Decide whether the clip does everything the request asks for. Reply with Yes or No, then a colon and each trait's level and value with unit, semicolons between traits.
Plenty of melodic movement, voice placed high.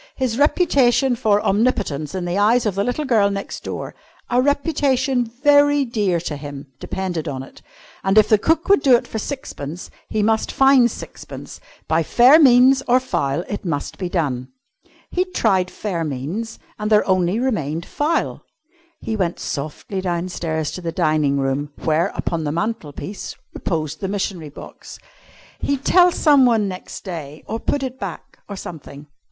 Yes: wide, 7.6 semitones; high, 200 Hz